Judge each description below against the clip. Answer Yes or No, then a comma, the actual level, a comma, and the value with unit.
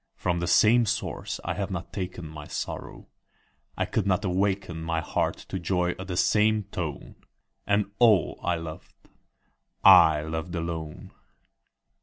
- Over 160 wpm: No, average, 145 wpm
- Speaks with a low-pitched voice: Yes, very low, 90 Hz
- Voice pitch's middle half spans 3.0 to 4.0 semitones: Yes, average, 3.4 semitones